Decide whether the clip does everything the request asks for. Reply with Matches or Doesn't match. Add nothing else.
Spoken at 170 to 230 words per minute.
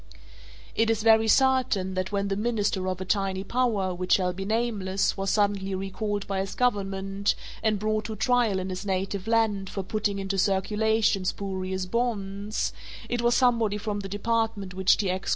Matches